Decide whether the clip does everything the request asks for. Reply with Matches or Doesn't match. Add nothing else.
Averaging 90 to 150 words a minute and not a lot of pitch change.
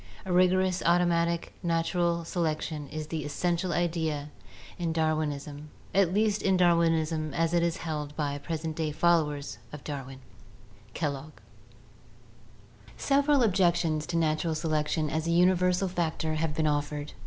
Matches